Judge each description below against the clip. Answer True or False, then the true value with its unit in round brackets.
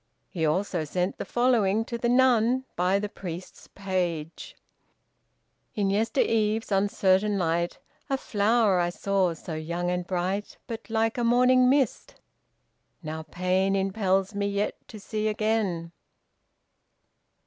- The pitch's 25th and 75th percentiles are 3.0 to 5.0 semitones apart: True (3.8 semitones)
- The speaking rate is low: True (130 wpm)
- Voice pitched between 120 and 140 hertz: False (200 Hz)